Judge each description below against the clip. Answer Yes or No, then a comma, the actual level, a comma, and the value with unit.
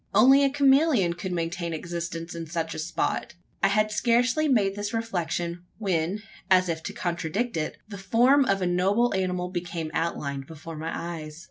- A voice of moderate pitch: Yes, medium, 180 Hz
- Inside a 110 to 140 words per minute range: No, average, 170 wpm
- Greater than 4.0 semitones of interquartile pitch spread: Yes, average, 4.6 semitones